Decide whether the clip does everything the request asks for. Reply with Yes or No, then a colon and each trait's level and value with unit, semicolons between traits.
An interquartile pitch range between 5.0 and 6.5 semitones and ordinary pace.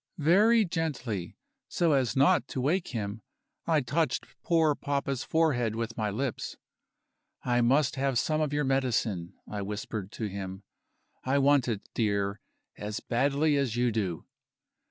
Yes: wide, 5.4 semitones; average, 145 wpm